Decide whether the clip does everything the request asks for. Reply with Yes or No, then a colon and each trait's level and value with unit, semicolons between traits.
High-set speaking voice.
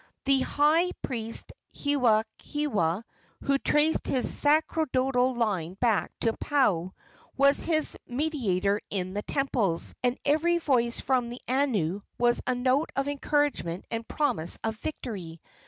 Yes: very high, 250 Hz